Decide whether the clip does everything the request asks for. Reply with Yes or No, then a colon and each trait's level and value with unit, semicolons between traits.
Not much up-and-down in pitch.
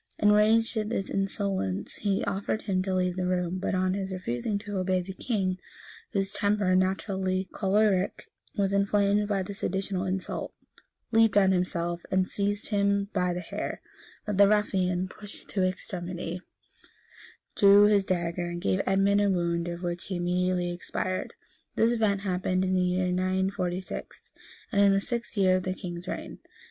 Yes: narrow, 1.8 semitones